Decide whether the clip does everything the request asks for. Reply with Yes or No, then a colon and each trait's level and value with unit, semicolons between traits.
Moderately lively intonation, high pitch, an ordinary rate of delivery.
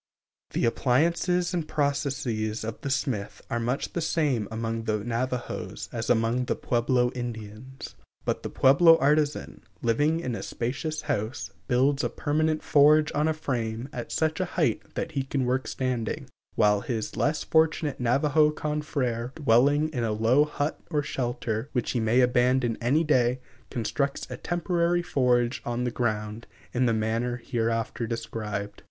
No: average, 4.4 semitones; low, 125 Hz; average, 155 wpm